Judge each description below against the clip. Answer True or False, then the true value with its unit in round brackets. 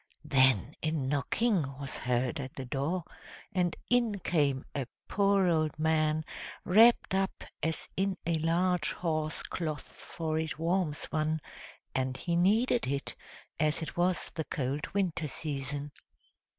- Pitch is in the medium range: True (155 Hz)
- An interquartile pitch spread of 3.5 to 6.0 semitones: True (4.1 semitones)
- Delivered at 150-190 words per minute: False (135 wpm)